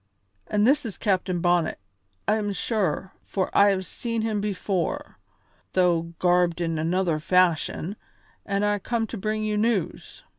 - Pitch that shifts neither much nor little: Yes, average, 3.3 semitones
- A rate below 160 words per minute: Yes, average, 150 wpm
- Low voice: No, high, 195 Hz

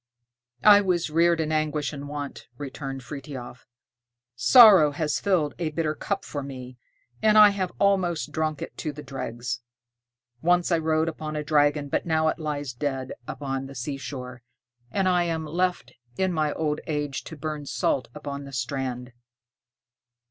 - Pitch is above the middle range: No, medium, 150 Hz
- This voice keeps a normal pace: Yes, average, 160 wpm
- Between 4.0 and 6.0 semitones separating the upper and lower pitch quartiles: No, average, 3.1 semitones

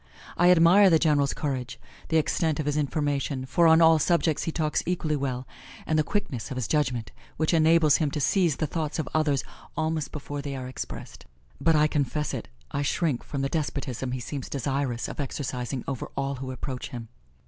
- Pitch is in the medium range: Yes, medium, 145 Hz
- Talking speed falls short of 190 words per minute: No, average, 195 wpm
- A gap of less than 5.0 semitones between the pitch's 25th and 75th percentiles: Yes, average, 3.1 semitones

